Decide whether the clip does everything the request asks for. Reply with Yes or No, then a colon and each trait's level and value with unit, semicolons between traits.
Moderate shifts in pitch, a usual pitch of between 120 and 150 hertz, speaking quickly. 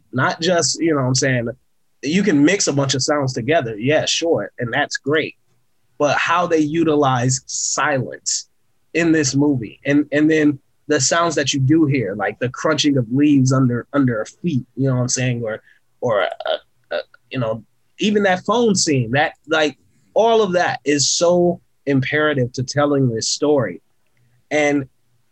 No: average, 3.6 semitones; medium, 140 Hz; average, 180 wpm